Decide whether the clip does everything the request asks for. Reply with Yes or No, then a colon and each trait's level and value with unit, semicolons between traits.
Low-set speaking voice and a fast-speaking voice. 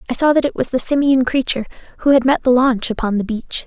No: very high, 255 Hz; fast, 260 wpm